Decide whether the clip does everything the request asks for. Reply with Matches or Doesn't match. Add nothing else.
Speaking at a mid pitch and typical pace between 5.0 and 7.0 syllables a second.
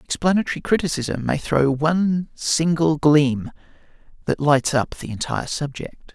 Doesn't match